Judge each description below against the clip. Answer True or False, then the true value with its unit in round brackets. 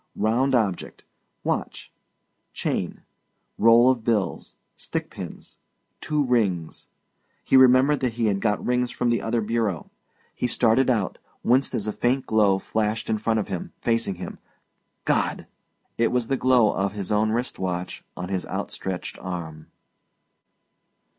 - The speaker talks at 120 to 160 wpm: True (145 wpm)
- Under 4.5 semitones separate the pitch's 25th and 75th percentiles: True (3.9 semitones)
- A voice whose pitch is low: True (110 Hz)